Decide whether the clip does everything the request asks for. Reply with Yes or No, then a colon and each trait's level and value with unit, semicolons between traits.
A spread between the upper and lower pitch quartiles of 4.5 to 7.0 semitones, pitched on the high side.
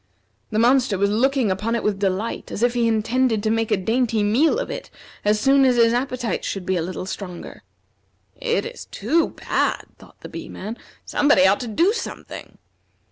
No: average, 4.0 semitones; high, 225 Hz